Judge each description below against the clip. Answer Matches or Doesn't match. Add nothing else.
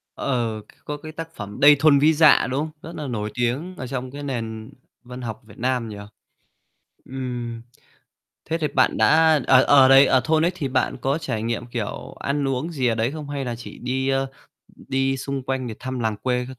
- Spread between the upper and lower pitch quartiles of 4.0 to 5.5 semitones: Doesn't match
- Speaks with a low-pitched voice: Matches